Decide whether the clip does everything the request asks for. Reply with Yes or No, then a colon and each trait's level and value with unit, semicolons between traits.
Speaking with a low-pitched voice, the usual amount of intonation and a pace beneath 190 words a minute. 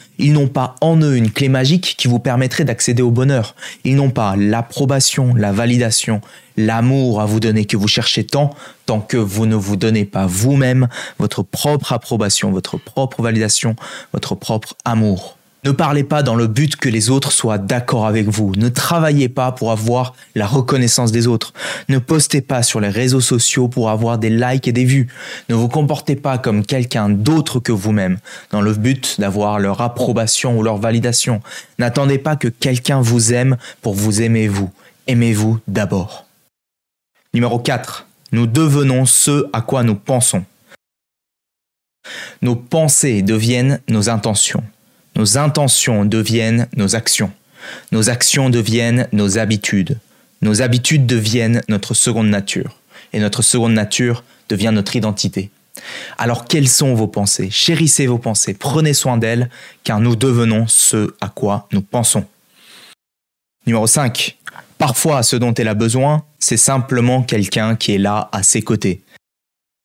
Yes: low, 120 Hz; average, 3.4 semitones; average, 160 wpm